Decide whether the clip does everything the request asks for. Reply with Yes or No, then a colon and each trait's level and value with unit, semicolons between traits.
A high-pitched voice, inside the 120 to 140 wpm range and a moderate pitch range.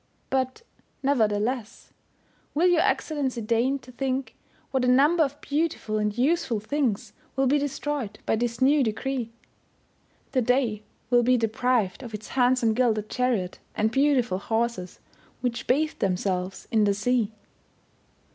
Yes: very high, 250 Hz; slow, 135 wpm; average, 3.7 semitones